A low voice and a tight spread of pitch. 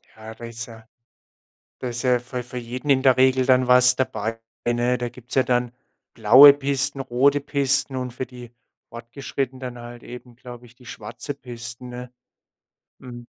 Yes: low, 125 Hz; narrow, 1.5 semitones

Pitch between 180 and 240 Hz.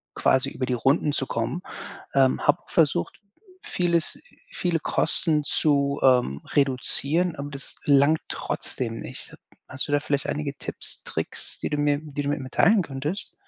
No: medium, 145 Hz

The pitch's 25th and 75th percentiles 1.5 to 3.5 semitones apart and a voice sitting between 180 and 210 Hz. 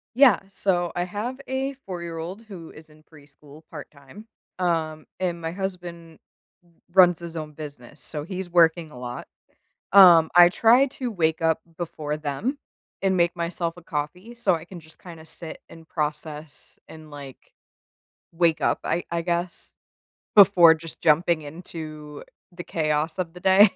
No: average, 2.7 semitones; medium, 170 Hz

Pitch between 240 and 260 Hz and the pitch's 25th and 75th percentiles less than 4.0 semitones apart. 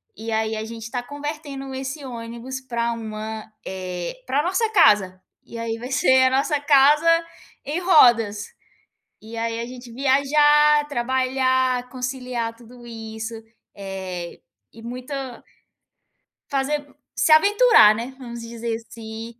Yes: high, 245 Hz; average, 3.3 semitones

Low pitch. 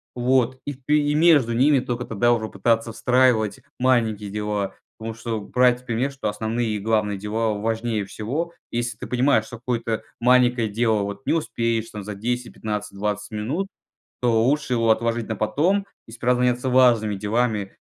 Yes: low, 115 Hz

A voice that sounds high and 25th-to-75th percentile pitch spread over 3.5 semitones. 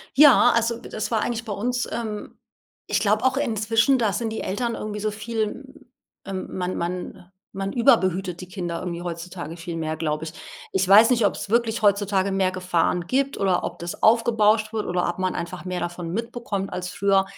Yes: high, 200 Hz; average, 4.0 semitones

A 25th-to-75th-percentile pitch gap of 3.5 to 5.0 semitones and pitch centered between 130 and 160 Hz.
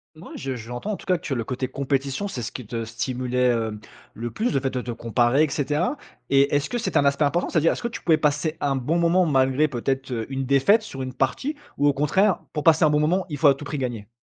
Yes: average, 3.8 semitones; medium, 140 Hz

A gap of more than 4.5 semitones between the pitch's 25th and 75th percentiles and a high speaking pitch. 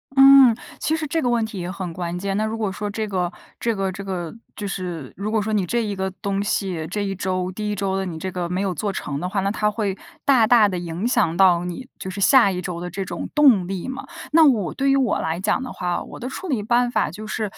No: average, 3.7 semitones; high, 200 Hz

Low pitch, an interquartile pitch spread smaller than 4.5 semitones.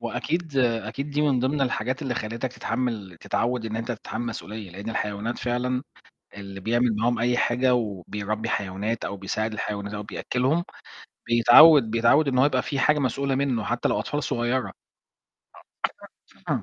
Yes: low, 120 Hz; average, 3.2 semitones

